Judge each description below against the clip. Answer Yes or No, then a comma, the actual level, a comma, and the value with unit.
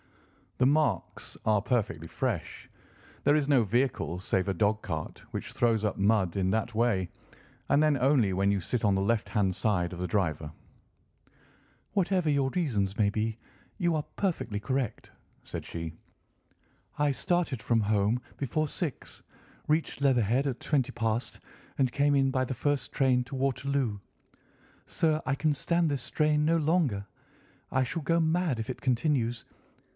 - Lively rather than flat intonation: Yes, wide, 5.8 semitones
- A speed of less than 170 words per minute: Yes, average, 160 wpm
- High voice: No, low, 125 Hz